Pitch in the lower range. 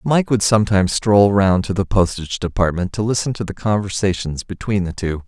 Yes: low, 100 Hz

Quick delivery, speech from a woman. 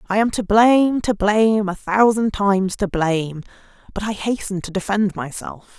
No: average, 175 wpm; female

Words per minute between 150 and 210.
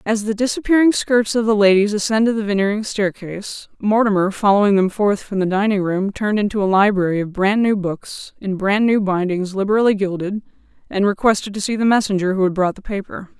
Yes: average, 195 wpm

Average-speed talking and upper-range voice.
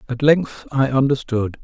No: average, 145 wpm; low, 135 Hz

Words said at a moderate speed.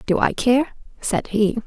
Yes: average, 180 wpm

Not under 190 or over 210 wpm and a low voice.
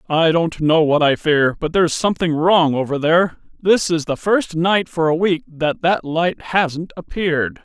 No: average, 195 wpm; medium, 165 Hz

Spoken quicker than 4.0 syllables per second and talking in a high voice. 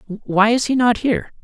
Yes: 5.0 syllables/s; high, 215 Hz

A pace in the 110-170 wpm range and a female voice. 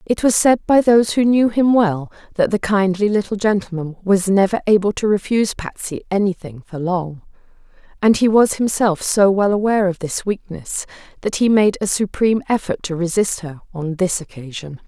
No: average, 180 wpm; female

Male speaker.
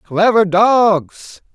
Yes: male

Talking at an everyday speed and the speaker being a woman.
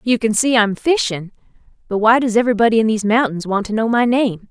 No: fast, 225 wpm; female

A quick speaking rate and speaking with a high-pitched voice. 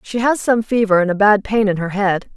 Yes: fast, 280 wpm; high, 205 Hz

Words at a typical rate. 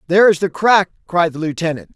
No: fast, 215 wpm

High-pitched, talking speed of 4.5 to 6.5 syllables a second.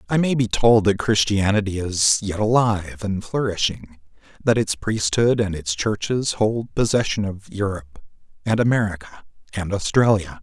No: low, 105 Hz; 4.6 syllables/s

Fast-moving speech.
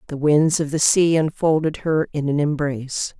No: average, 190 wpm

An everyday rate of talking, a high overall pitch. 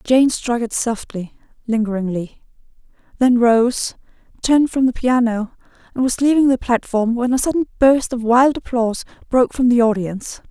Yes: average, 155 wpm; high, 240 Hz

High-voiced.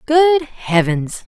Yes: very high, 250 Hz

